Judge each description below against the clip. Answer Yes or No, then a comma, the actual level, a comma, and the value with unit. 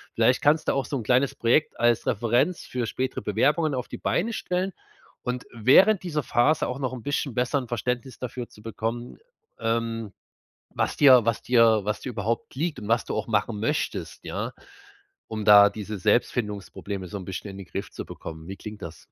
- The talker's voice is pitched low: Yes, low, 120 Hz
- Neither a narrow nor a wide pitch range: Yes, average, 3.8 semitones